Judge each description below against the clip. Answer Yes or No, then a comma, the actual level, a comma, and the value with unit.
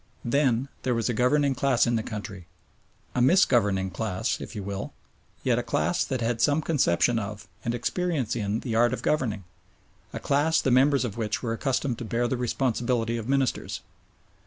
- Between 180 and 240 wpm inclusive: Yes, average, 185 wpm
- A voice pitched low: Yes, low, 120 Hz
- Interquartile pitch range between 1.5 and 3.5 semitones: Yes, average, 3.2 semitones